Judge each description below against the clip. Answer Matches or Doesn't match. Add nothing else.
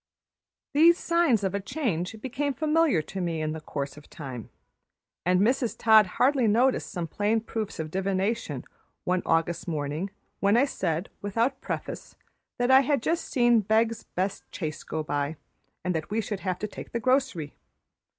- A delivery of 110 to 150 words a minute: Doesn't match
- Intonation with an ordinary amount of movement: Doesn't match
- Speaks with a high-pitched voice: Matches